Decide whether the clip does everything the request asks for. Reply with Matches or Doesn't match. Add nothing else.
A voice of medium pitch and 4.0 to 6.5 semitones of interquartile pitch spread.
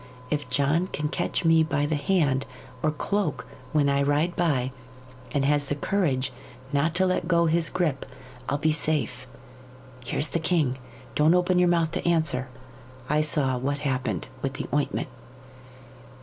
Doesn't match